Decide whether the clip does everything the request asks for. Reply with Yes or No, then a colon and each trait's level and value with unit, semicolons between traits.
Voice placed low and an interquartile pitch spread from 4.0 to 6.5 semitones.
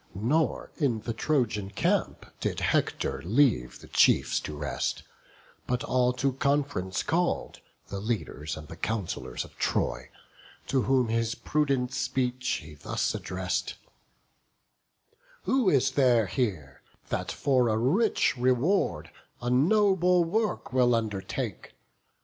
Yes: low, 125 Hz; average, 5.2 semitones